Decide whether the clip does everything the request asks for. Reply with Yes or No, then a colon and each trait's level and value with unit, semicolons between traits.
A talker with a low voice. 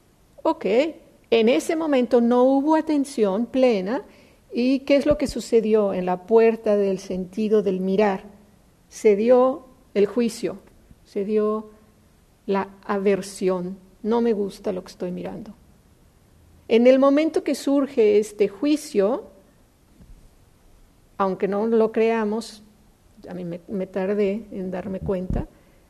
No: high, 215 Hz